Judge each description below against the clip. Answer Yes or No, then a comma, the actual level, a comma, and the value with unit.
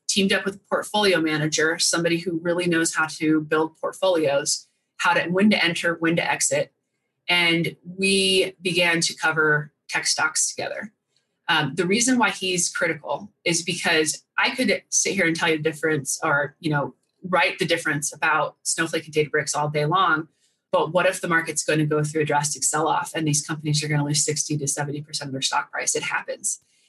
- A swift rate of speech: No, average, 190 wpm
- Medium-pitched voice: Yes, medium, 165 Hz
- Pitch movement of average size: Yes, average, 3.1 semitones